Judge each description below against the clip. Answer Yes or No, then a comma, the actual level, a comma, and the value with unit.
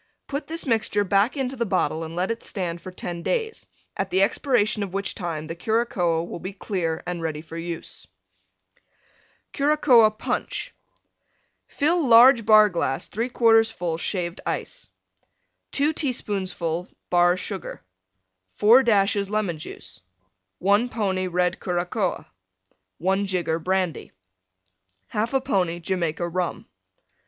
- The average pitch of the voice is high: Yes, high, 195 Hz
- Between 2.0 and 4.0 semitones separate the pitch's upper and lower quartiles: No, average, 4.7 semitones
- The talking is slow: Yes, slow, 130 wpm